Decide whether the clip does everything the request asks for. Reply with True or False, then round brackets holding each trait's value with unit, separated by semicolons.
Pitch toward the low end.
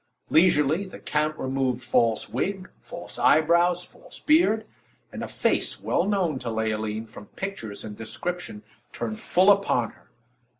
False (150 Hz)